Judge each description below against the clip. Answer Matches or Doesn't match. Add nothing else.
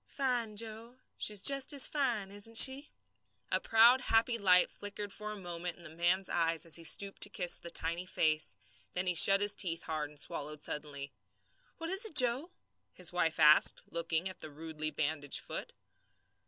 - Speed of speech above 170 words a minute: Matches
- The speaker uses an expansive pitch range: Matches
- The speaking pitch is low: Doesn't match